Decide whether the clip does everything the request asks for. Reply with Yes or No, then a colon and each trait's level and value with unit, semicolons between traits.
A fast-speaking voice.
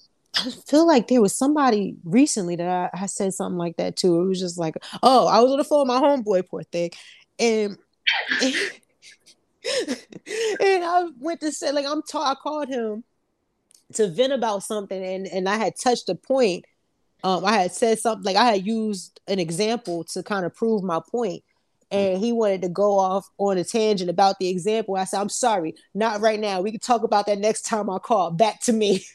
Yes: fast, 210 wpm